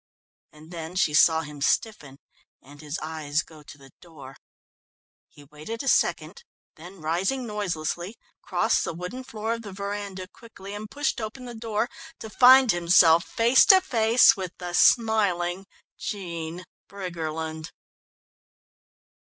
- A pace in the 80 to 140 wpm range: Yes, slow, 135 wpm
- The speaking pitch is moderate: Yes, medium, 180 Hz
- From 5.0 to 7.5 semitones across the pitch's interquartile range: Yes, wide, 5.5 semitones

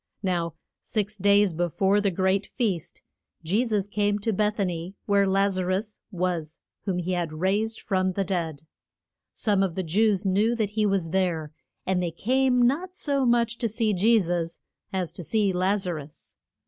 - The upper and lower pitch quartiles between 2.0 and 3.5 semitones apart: Yes, average, 3.0 semitones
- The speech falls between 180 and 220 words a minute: Yes, average, 185 wpm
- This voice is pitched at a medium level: No, high, 195 Hz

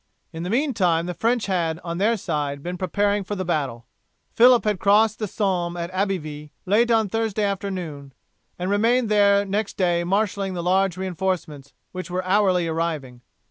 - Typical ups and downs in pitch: Yes, average, 3.2 semitones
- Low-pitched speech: No, medium, 185 Hz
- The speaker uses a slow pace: No, average, 170 wpm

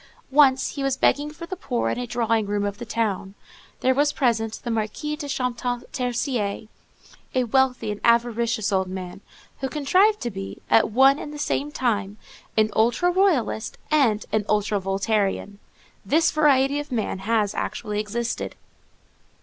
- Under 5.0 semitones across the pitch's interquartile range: Yes, average, 4.5 semitones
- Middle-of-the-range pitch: No, high, 235 Hz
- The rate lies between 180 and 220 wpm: No, average, 160 wpm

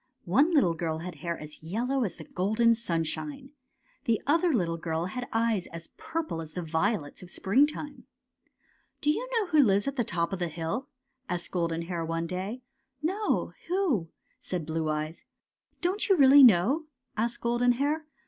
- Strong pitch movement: Yes, wide, 8.5 semitones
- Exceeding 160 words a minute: Yes, average, 190 wpm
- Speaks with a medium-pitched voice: No, high, 215 Hz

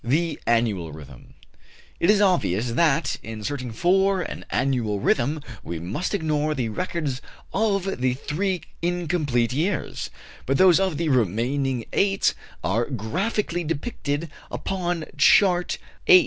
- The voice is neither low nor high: Yes, medium, 150 Hz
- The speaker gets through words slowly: Yes, slow, 130 wpm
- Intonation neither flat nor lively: No, wide, 7.0 semitones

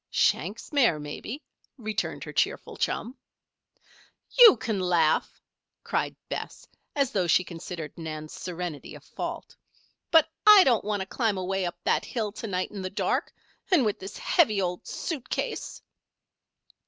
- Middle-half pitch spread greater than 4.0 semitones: Yes, average, 5.2 semitones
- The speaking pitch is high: Yes, high, 200 Hz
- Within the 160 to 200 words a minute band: No, average, 150 wpm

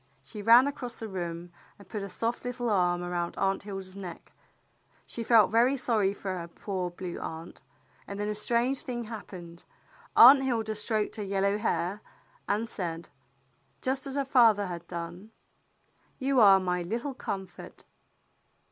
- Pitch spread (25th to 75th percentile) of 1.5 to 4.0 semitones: No, average, 4.5 semitones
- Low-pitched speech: No, high, 205 Hz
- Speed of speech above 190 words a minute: No, average, 165 wpm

